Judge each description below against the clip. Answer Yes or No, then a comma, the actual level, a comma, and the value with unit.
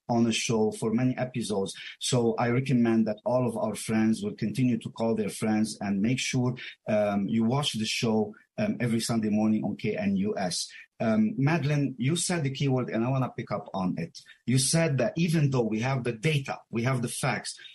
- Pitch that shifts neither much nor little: Yes, average, 4.1 semitones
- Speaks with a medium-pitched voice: No, low, 120 Hz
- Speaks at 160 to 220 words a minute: Yes, fast, 205 wpm